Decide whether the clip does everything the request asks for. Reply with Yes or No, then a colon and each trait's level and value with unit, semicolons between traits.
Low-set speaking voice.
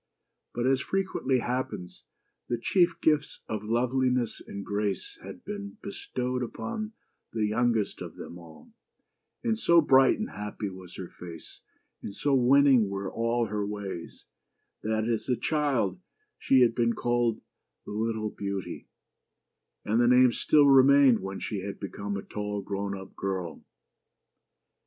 Yes: low, 115 Hz